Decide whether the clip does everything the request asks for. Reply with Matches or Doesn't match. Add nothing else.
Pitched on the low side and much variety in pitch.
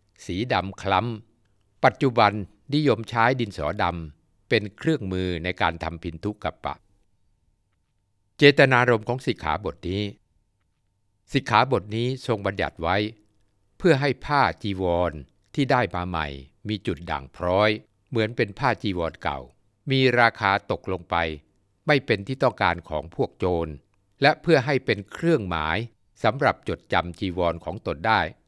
Doesn't match